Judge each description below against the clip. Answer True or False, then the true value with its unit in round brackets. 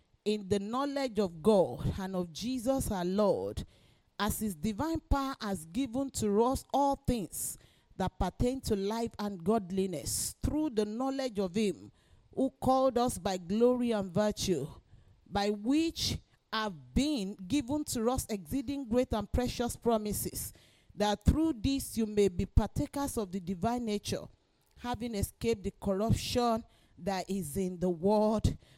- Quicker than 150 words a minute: False (145 wpm)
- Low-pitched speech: False (215 Hz)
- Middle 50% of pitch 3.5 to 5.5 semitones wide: True (4.4 semitones)